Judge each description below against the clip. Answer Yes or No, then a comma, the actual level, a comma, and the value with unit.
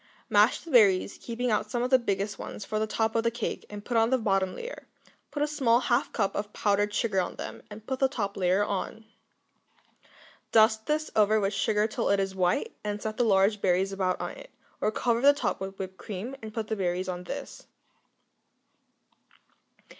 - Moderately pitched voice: No, high, 215 Hz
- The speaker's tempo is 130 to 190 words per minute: No, fast, 205 wpm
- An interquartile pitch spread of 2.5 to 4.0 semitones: Yes, average, 3.3 semitones